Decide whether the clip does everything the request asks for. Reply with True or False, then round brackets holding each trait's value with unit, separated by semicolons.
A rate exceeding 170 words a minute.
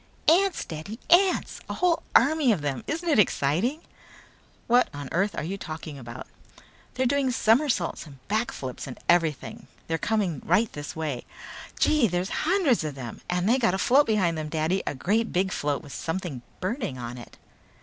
True (180 wpm)